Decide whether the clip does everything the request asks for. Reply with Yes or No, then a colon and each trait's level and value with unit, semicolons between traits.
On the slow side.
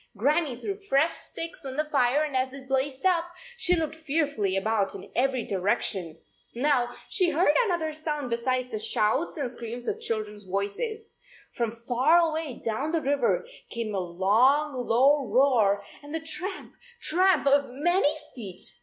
No: average, 165 wpm